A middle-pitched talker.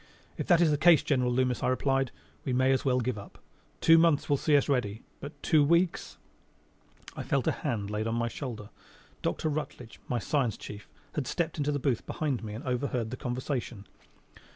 No: low, 130 Hz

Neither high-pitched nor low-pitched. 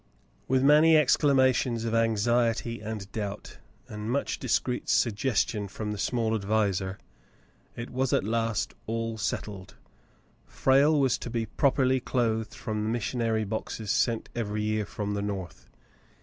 No: low, 115 Hz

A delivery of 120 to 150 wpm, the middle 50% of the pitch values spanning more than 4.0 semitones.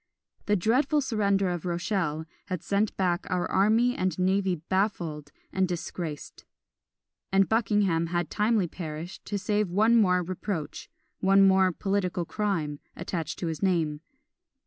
No: slow, 135 wpm; average, 3.1 semitones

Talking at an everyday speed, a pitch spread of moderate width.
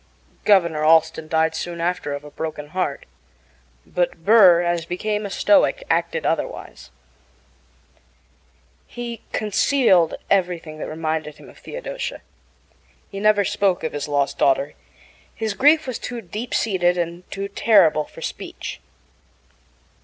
No: slow, 130 wpm; average, 5.0 semitones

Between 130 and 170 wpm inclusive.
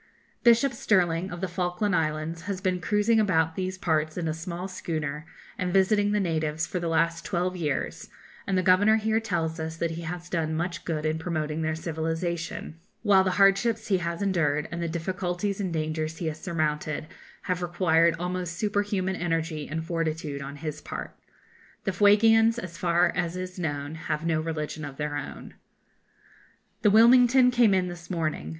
No: average, 180 wpm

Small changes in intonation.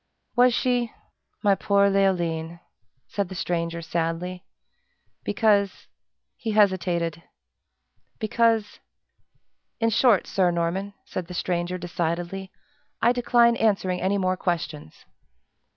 No: average, 3.5 semitones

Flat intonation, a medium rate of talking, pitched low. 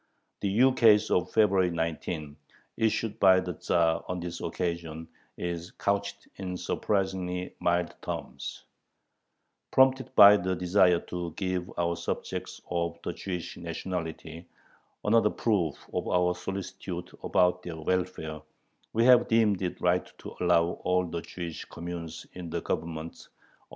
No: narrow, 2.3 semitones; slow, 130 wpm; very low, 90 Hz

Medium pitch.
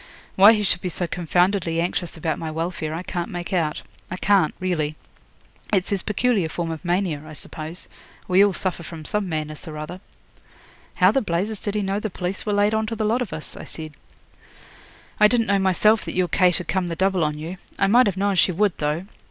Yes: medium, 180 Hz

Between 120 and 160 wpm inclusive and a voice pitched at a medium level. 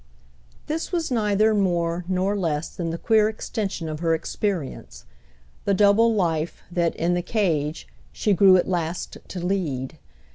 Yes: average, 150 wpm; medium, 180 Hz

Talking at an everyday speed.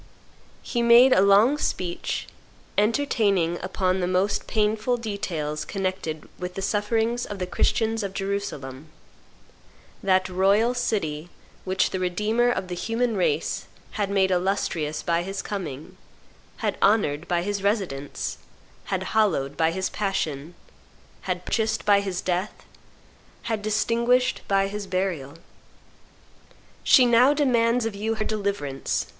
No: slow, 130 wpm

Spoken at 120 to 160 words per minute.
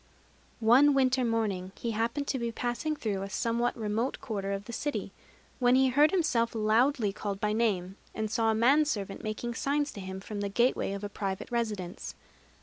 No: average, 190 wpm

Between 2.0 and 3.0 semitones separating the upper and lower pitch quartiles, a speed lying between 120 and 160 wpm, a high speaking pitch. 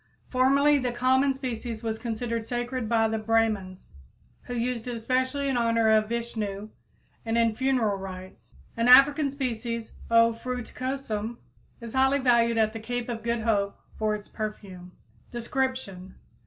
Yes: narrow, 2.6 semitones; average, 145 wpm; high, 230 Hz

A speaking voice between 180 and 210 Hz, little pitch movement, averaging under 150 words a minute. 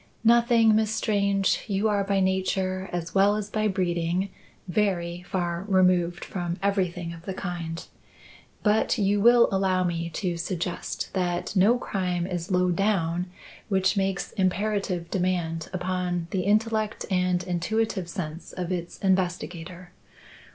Yes: medium, 185 Hz; narrow, 2.2 semitones; slow, 135 wpm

